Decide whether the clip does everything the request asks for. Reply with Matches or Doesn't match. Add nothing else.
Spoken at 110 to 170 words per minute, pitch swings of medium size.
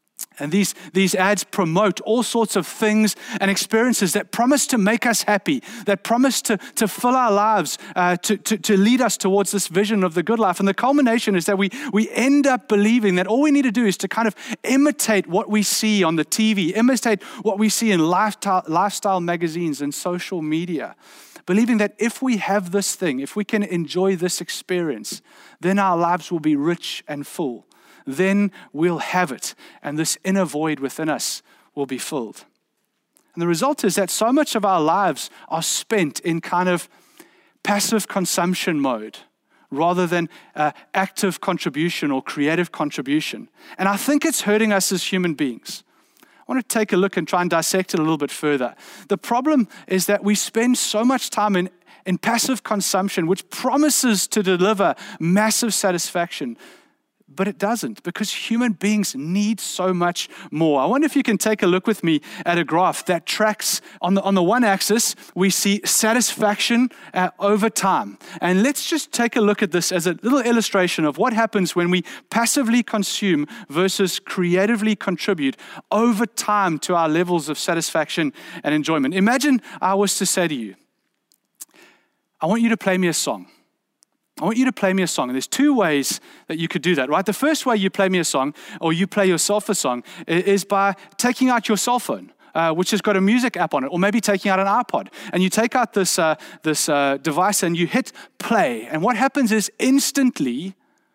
Doesn't match